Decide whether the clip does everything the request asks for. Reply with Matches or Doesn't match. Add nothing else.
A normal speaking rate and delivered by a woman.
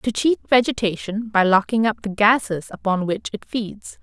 Matches